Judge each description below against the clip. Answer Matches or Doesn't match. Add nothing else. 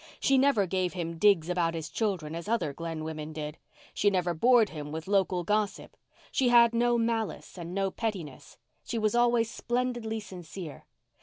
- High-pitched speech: Matches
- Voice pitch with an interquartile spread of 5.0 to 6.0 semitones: Matches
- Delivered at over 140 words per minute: Matches